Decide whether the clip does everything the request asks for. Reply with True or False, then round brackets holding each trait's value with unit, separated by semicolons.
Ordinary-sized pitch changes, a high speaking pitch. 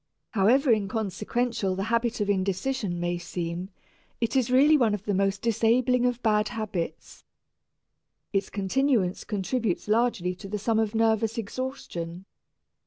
True (3.7 semitones; 215 Hz)